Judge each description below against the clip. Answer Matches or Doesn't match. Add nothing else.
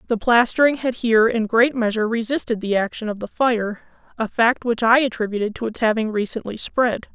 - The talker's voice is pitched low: Doesn't match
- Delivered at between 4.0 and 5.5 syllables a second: Doesn't match